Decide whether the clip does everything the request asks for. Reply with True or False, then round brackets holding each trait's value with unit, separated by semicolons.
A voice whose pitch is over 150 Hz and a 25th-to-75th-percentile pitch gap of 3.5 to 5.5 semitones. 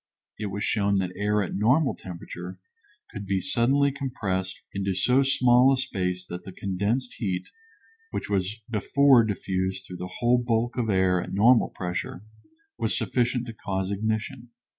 False (105 Hz; 4.5 semitones)